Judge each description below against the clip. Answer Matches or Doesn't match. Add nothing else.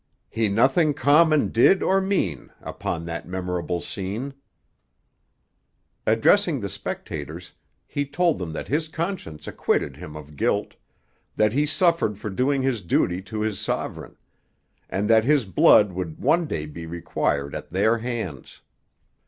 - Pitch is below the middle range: Matches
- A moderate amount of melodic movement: Doesn't match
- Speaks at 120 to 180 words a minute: Matches